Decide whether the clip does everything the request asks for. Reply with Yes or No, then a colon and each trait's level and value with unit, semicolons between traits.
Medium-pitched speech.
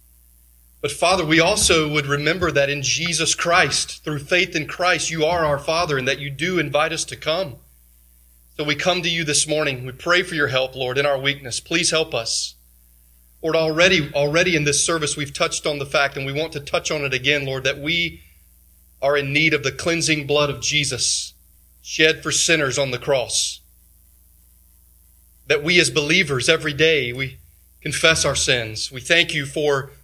Yes: medium, 145 Hz